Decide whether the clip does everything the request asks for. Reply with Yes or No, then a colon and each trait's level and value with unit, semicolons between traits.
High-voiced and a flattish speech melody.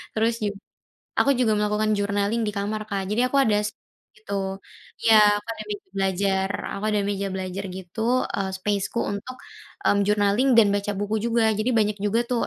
Yes: high, 205 Hz; narrow, 1.5 semitones